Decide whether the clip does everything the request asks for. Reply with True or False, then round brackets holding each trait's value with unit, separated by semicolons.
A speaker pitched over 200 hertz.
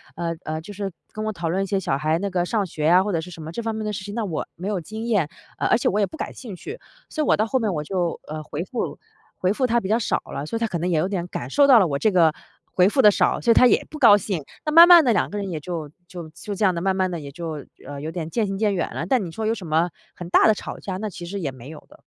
False (190 Hz)